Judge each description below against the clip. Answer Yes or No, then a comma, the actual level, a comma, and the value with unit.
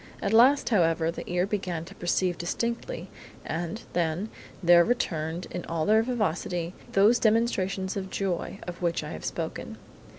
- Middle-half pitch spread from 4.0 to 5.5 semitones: Yes, average, 4.3 semitones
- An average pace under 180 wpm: Yes, average, 155 wpm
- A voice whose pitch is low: No, medium, 185 Hz